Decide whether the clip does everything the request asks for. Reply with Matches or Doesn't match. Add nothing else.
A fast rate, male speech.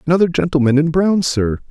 Doesn't match